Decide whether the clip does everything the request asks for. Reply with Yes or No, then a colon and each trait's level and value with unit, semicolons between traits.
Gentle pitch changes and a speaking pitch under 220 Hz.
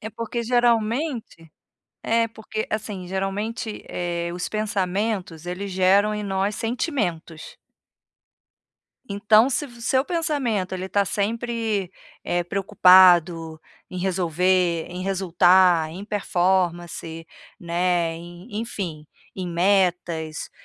No: average, 3.7 semitones; high, 190 Hz